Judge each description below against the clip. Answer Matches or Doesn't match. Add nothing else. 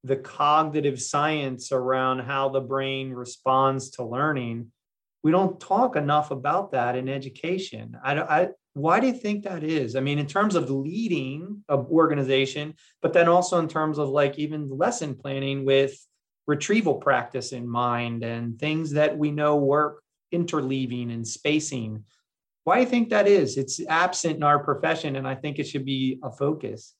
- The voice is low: Doesn't match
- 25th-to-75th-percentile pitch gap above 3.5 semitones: Doesn't match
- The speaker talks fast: Doesn't match